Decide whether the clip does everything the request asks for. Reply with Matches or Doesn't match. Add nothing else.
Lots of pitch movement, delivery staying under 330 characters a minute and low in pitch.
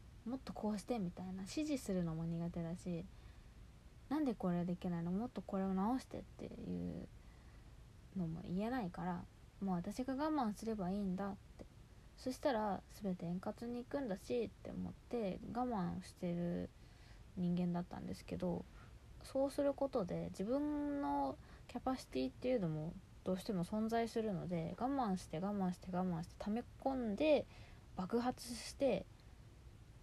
Doesn't match